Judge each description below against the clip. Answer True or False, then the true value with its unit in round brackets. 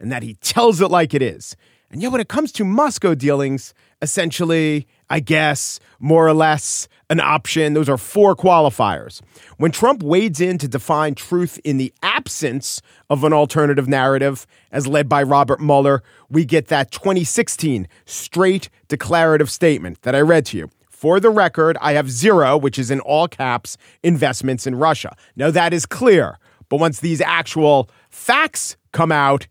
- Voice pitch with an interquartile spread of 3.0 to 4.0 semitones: True (3.7 semitones)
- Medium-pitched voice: True (150 Hz)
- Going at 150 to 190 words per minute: True (170 wpm)